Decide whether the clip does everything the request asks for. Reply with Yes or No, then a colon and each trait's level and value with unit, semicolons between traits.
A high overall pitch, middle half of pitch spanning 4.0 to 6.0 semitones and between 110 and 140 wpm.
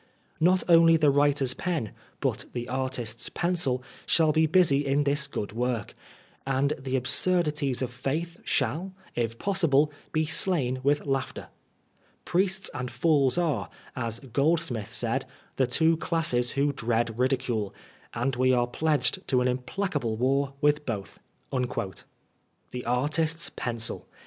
No: low, 135 Hz; average, 4.4 semitones; slow, 135 wpm